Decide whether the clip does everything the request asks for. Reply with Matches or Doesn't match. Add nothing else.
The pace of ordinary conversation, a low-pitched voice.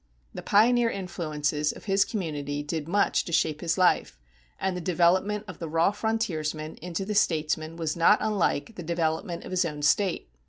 Doesn't match